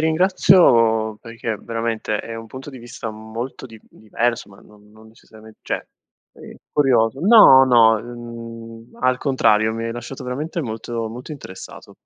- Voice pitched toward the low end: Yes, low, 115 Hz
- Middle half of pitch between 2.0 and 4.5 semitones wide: Yes, average, 2.7 semitones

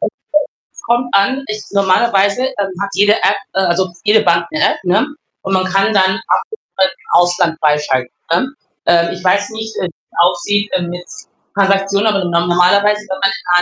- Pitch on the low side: No, high, 195 Hz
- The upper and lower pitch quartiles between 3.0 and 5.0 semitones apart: No, narrow, 2.5 semitones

